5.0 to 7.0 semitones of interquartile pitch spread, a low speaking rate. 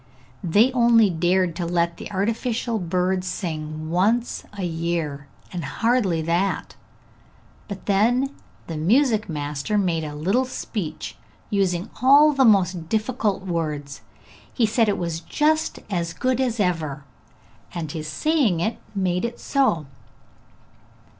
Yes: wide, 5.6 semitones; slow, 130 wpm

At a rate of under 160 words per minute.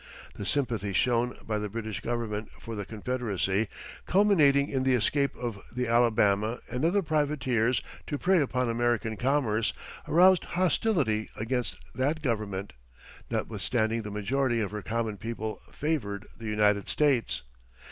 Yes: slow, 135 wpm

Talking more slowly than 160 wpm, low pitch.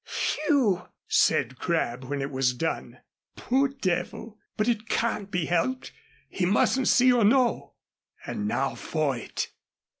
No: average, 140 wpm; high, 195 Hz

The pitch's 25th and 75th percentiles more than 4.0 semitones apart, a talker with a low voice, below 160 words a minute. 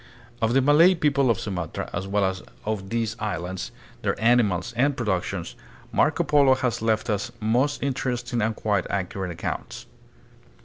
Yes: average, 4.7 semitones; low, 110 Hz; average, 150 wpm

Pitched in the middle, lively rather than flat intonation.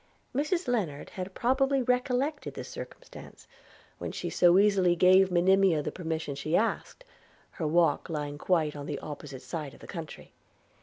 Yes: medium, 180 Hz; wide, 7.7 semitones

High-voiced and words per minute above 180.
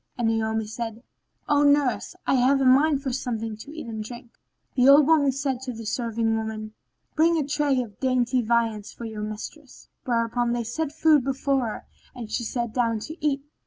Yes: high, 245 Hz; average, 195 wpm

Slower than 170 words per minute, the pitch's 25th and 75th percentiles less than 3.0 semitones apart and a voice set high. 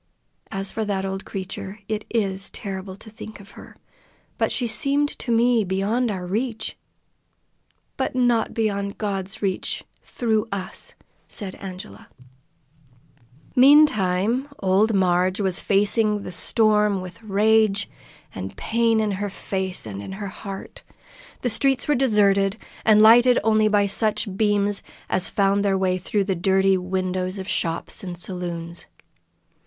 Yes: average, 140 wpm; narrow, 2.5 semitones; high, 200 Hz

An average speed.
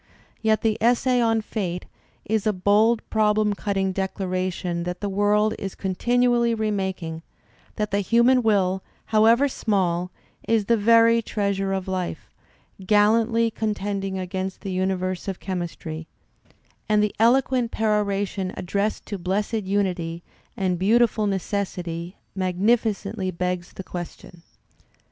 No: slow, 125 wpm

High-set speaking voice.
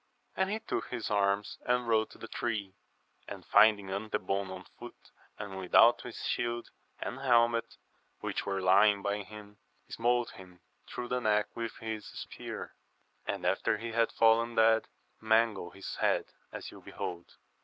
No: low, 110 Hz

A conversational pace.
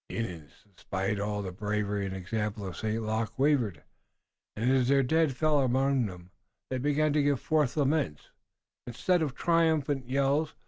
Yes: average, 165 wpm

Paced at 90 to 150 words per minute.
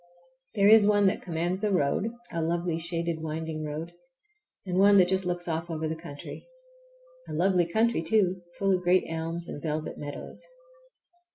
No: average, 170 wpm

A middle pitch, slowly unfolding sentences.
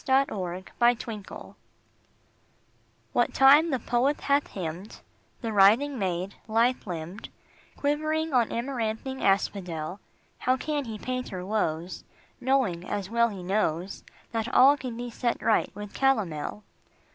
No: high, 225 Hz; slow, 125 wpm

